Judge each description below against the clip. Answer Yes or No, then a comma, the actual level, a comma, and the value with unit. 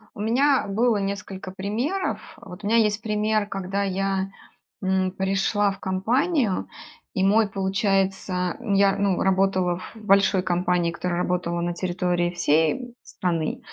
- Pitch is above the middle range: Yes, high, 195 Hz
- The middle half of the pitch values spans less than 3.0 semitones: Yes, narrow, 2.4 semitones